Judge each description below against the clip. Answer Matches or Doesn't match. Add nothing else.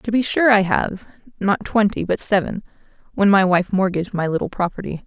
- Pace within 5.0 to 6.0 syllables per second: Matches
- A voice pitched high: Matches